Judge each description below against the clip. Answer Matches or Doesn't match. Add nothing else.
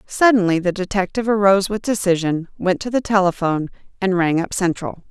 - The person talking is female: Matches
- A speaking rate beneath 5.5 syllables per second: Doesn't match